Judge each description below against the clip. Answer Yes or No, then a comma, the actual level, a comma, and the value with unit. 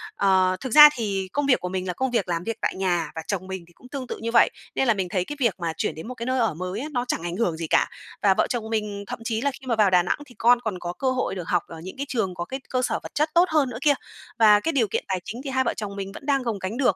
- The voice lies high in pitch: Yes, high, 215 Hz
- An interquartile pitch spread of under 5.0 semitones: No, wide, 5.5 semitones